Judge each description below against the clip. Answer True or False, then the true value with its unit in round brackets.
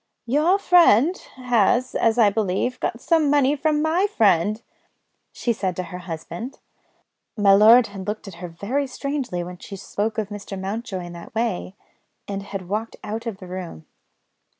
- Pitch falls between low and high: False (215 Hz)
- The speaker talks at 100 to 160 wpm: False (170 wpm)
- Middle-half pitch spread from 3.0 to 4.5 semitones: False (5.0 semitones)